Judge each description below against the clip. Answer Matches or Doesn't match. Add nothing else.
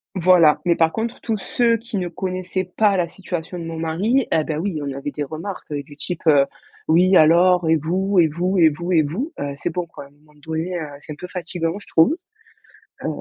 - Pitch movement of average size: Matches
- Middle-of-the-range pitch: Matches